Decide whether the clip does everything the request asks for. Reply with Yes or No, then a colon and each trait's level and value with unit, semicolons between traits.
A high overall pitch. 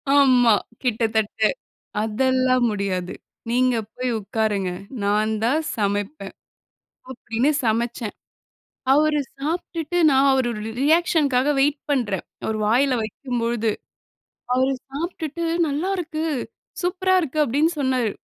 Yes: very high, 255 Hz